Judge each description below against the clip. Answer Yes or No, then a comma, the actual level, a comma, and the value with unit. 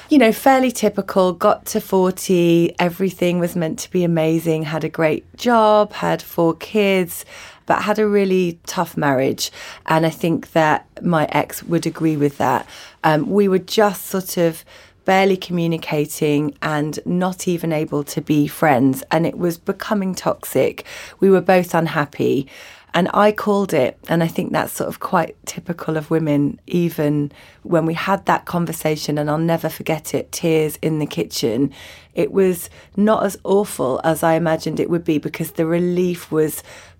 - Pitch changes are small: No, average, 3.3 semitones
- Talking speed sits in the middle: Yes, average, 170 wpm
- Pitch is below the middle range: No, medium, 170 Hz